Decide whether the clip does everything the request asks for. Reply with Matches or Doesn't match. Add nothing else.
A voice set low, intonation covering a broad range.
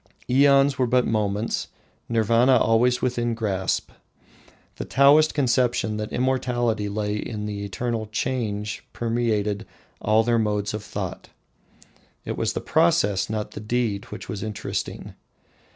Doesn't match